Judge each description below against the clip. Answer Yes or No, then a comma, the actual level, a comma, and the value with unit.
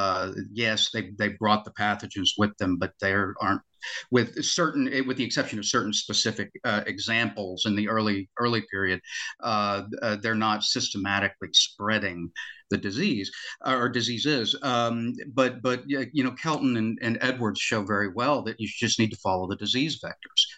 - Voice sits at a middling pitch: No, low, 110 Hz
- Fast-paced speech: No, average, 170 wpm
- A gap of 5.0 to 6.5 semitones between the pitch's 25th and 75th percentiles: No, average, 3.3 semitones